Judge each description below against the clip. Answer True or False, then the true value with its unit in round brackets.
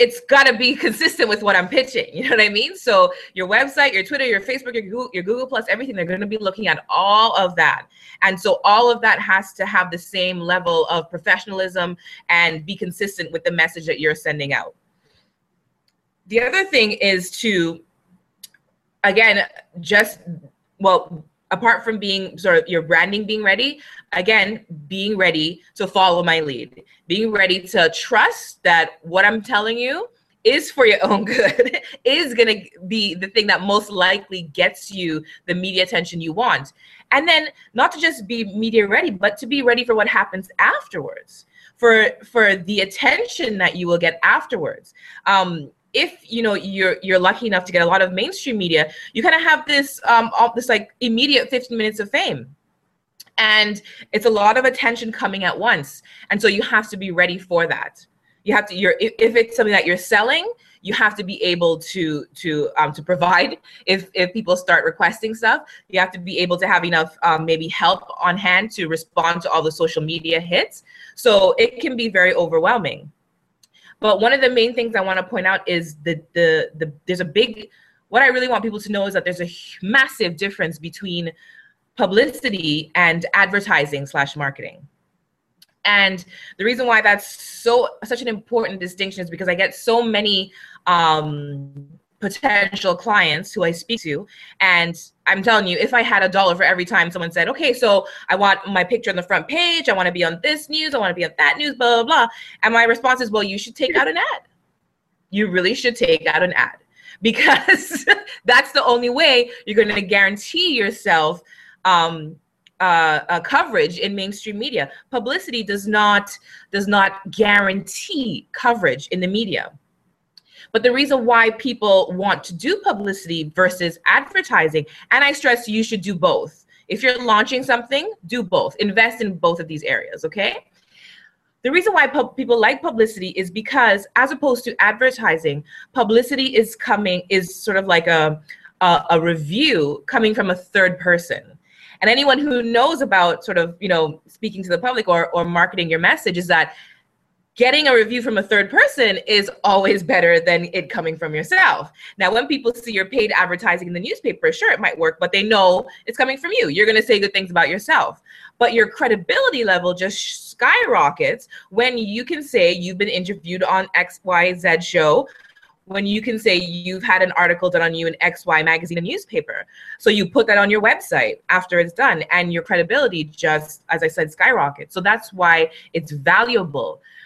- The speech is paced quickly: False (190 wpm)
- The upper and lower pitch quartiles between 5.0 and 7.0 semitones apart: True (5.5 semitones)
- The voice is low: False (205 Hz)